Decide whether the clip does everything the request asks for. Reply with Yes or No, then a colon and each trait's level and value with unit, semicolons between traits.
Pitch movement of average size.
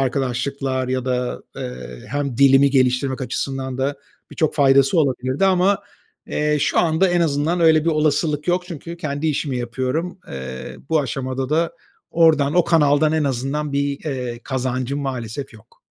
Yes: average, 3.2 semitones